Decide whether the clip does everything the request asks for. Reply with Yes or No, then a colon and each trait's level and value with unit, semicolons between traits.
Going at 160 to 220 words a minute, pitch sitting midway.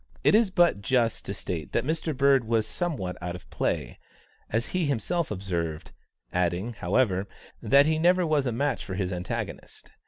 No: average, 175 wpm; low, 115 Hz